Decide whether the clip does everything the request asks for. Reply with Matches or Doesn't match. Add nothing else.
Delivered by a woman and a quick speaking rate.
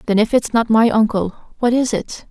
Matches